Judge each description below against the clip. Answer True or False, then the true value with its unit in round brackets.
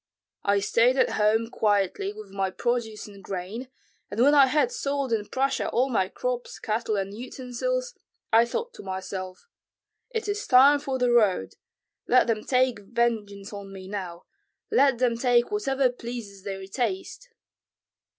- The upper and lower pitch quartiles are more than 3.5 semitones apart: True (4.6 semitones)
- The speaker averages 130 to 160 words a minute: True (155 wpm)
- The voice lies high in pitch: True (235 Hz)